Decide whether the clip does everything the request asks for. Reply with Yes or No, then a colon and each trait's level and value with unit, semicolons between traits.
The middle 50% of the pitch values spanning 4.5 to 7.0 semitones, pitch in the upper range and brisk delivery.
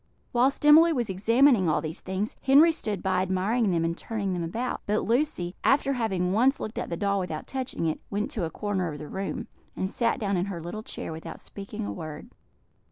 Yes: average, 5.0 semitones; high, 200 Hz; fast, 215 wpm